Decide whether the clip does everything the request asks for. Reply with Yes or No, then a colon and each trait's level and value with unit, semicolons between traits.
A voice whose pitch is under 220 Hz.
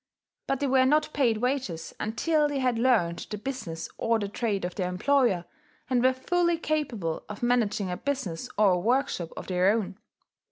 No: high, 230 Hz